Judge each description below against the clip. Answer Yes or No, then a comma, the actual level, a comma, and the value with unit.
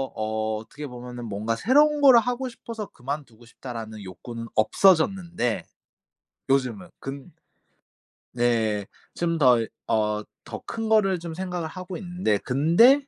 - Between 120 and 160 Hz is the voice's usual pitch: Yes, low, 135 Hz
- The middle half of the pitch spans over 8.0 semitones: Yes, wide, 8.6 semitones